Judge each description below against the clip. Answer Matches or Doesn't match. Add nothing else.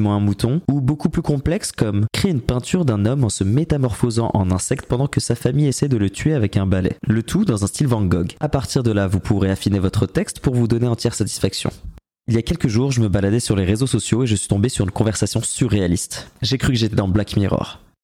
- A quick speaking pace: Matches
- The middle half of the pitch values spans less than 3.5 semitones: Doesn't match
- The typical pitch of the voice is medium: Doesn't match